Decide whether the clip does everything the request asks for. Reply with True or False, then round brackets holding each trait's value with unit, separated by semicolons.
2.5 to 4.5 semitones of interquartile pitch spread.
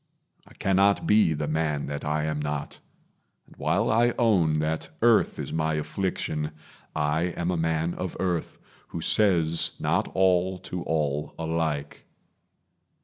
True (3.2 semitones)